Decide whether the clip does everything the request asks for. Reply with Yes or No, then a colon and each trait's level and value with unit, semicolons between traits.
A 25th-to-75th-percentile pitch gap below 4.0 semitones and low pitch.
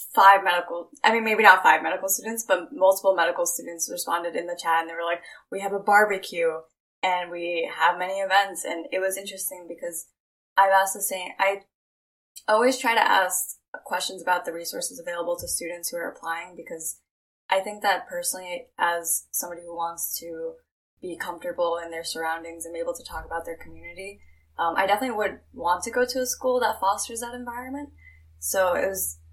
No: average, 2.9 semitones; medium, 180 Hz